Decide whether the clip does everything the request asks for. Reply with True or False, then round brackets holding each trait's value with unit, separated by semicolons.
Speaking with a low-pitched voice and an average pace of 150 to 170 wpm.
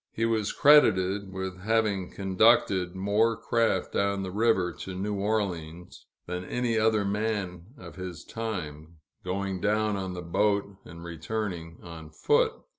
False (95 Hz; 140 wpm)